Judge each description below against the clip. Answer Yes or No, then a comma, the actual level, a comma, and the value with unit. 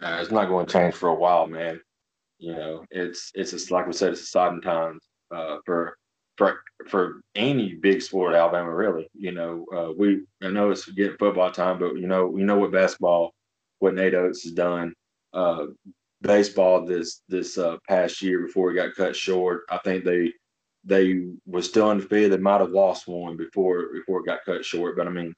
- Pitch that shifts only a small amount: Yes, narrow, 2.1 semitones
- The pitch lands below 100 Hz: Yes, very low, 90 Hz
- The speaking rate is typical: No, fast, 210 wpm